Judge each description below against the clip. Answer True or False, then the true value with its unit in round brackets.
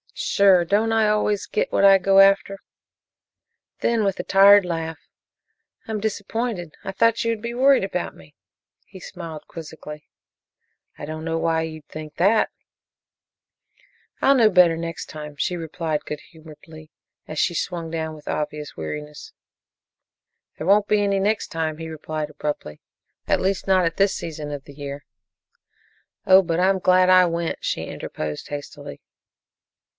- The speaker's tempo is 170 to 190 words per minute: False (155 wpm)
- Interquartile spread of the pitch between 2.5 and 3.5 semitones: False (4.1 semitones)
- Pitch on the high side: False (170 Hz)